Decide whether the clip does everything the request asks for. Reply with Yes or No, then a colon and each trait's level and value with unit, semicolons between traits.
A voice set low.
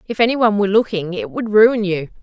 No: high, 205 Hz